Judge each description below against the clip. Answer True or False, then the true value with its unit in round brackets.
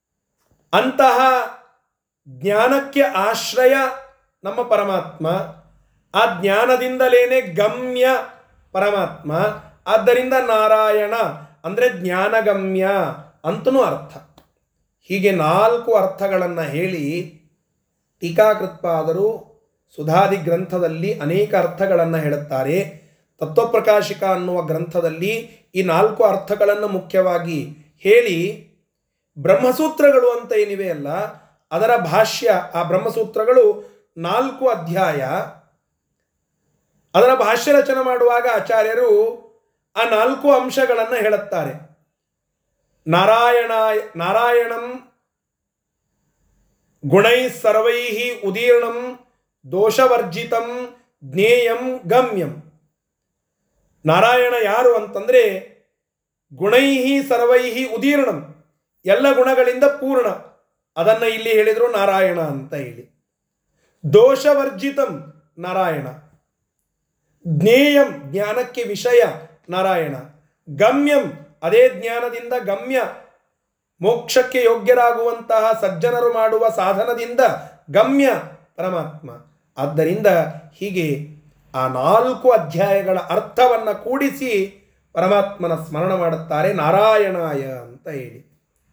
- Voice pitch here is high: True (215 Hz)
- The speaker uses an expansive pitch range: True (6.1 semitones)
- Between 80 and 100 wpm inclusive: False (70 wpm)